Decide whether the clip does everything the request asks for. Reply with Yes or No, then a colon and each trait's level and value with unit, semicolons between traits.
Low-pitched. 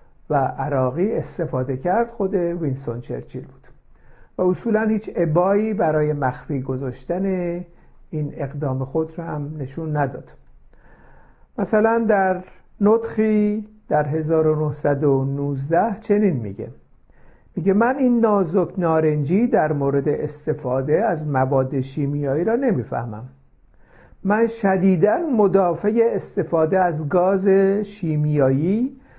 No: medium, 165 Hz